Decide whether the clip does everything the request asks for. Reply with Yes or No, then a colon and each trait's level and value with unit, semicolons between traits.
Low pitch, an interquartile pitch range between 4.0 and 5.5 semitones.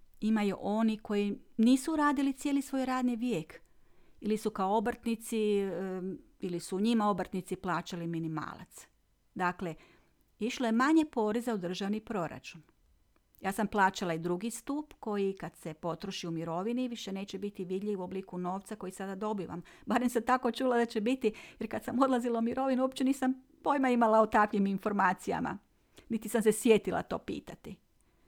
No: high, 215 Hz; average, 4.3 semitones